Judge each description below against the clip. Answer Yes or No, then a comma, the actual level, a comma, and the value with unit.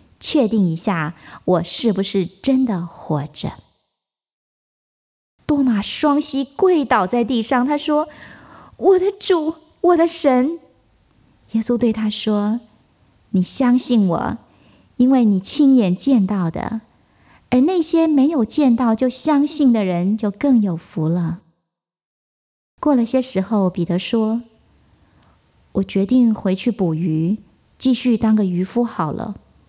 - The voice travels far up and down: Yes, wide, 6.0 semitones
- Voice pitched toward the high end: Yes, high, 230 Hz